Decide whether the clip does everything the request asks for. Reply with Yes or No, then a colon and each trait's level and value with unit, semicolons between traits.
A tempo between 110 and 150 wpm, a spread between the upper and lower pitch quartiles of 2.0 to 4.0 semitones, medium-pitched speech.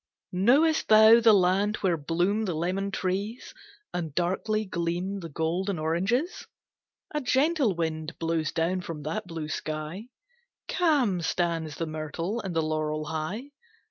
No: average, 140 wpm; average, 4.9 semitones; medium, 180 Hz